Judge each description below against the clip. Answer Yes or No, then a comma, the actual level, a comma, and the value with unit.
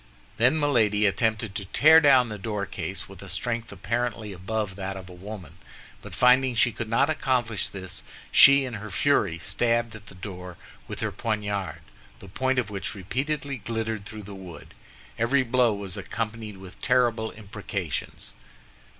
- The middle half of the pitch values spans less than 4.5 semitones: Yes, average, 3.8 semitones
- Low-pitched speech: Yes, low, 110 Hz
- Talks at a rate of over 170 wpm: No, average, 160 wpm